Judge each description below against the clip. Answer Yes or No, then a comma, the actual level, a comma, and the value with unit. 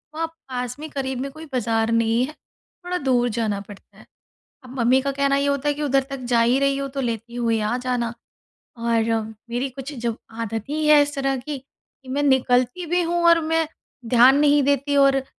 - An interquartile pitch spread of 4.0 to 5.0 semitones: No, average, 3.0 semitones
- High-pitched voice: Yes, very high, 270 Hz